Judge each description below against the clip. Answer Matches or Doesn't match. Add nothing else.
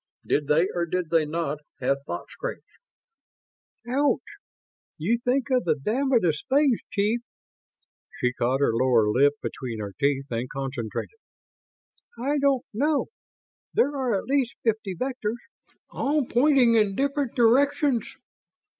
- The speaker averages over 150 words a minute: Doesn't match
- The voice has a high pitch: Matches